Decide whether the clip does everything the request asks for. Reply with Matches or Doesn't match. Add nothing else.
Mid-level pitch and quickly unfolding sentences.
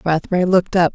Doesn't match